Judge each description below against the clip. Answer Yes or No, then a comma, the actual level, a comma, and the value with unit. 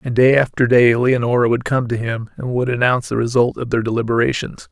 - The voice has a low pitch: Yes, low, 120 Hz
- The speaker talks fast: Yes, fast, 215 wpm